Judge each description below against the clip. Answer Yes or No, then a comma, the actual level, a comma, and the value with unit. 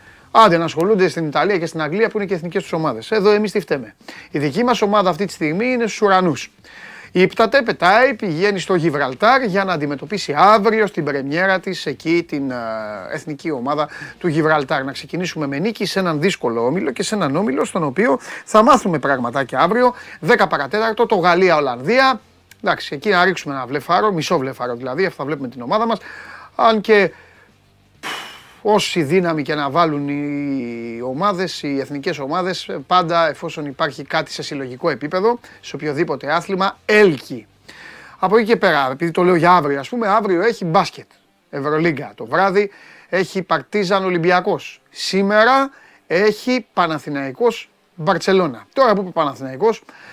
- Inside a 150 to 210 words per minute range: Yes, average, 165 wpm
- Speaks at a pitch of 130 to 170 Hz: No, medium, 180 Hz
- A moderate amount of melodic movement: No, wide, 5.7 semitones